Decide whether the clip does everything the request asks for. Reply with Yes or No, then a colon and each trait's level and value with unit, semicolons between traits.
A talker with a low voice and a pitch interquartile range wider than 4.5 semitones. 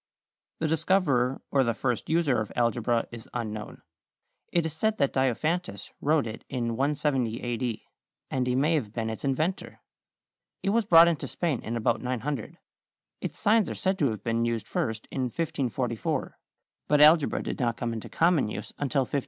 Yes: low, 130 Hz; average, 5.2 semitones